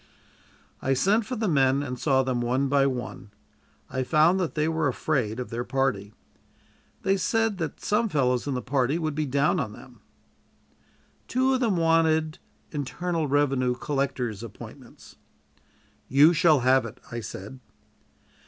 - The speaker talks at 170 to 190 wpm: No, average, 155 wpm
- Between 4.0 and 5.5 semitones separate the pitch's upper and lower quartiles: Yes, average, 4.4 semitones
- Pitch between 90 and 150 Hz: Yes, medium, 140 Hz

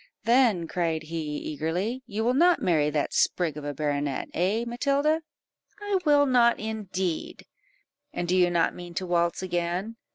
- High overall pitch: No, medium, 180 Hz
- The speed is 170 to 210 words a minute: No, average, 160 wpm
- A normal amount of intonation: No, wide, 6.4 semitones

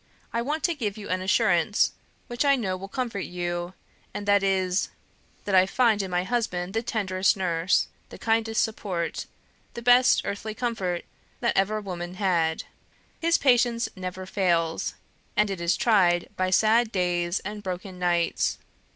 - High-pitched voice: Yes, high, 195 Hz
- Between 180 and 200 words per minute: No, average, 160 wpm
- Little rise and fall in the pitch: No, average, 3.8 semitones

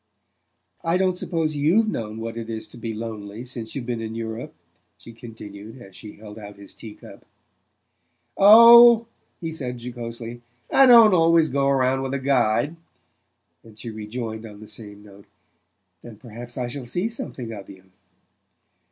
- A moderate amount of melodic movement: Yes, average, 5.0 semitones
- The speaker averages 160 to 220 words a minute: Yes, average, 165 wpm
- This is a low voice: Yes, low, 120 Hz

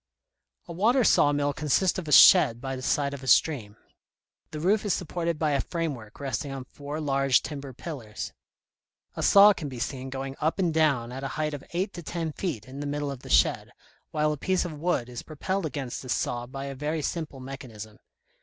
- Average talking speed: No, fast, 210 wpm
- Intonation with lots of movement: No, average, 3.5 semitones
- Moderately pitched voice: Yes, medium, 145 Hz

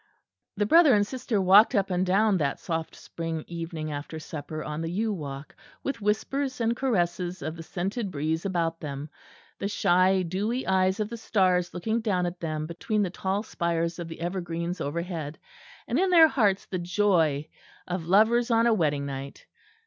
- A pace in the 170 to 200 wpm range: Yes, average, 180 wpm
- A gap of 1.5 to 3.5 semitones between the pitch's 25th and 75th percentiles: No, average, 4.2 semitones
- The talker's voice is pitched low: No, medium, 180 Hz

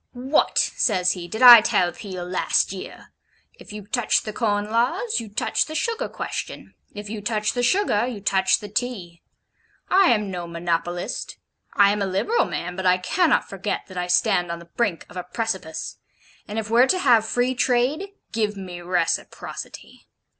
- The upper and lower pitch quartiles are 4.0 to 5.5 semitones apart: Yes, average, 5.0 semitones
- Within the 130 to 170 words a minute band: No, average, 180 wpm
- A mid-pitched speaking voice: No, high, 205 Hz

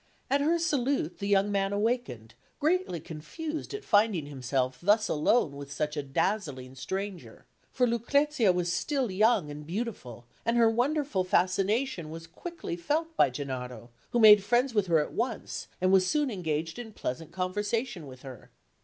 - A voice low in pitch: No, high, 195 Hz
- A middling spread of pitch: No, wide, 7.9 semitones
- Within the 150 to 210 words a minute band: Yes, average, 160 wpm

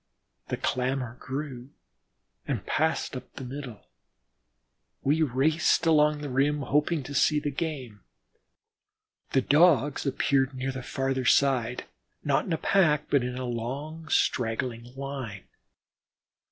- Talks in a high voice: No, low, 135 Hz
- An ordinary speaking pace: No, slow, 125 wpm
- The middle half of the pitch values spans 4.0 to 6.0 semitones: No, average, 2.8 semitones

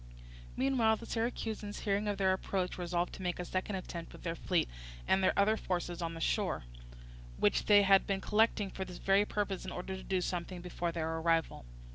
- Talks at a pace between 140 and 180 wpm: No, average, 195 wpm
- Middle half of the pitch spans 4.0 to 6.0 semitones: No, narrow, 2.6 semitones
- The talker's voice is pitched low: No, high, 190 Hz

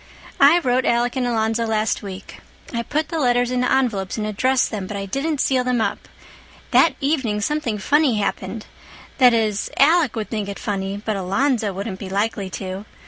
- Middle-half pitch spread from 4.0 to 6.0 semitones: Yes, average, 4.4 semitones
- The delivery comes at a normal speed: Yes, average, 185 wpm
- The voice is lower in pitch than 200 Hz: No, high, 225 Hz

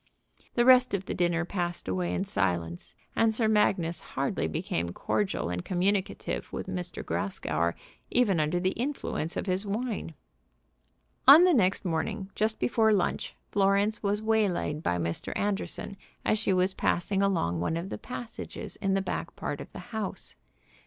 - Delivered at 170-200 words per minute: No, average, 160 wpm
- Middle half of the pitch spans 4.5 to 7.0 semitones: Yes, average, 4.8 semitones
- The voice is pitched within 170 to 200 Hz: Yes, high, 190 Hz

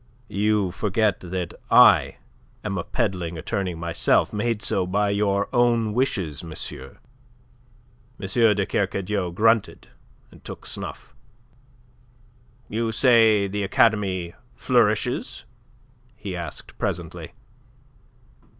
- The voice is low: Yes, low, 100 Hz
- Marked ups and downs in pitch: No, average, 3.3 semitones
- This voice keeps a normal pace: No, slow, 100 wpm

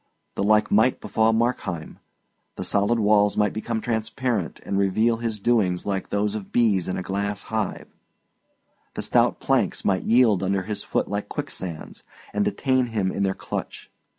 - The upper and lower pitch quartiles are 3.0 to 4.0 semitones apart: No, narrow, 2.4 semitones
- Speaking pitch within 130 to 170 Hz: No, low, 105 Hz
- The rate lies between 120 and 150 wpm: No, average, 165 wpm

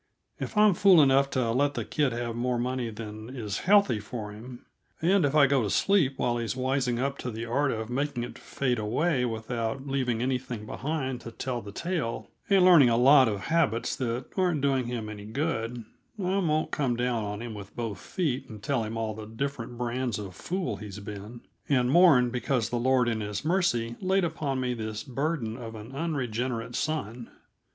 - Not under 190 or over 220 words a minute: Yes, average, 195 wpm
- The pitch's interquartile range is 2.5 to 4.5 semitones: Yes, average, 3.8 semitones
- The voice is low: Yes, low, 125 Hz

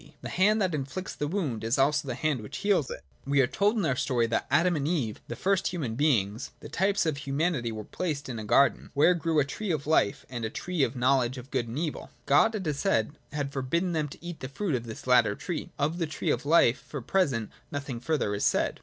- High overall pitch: No, medium, 145 Hz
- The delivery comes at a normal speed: No, fast, 260 wpm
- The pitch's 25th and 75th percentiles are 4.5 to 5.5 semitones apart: Yes, average, 5.2 semitones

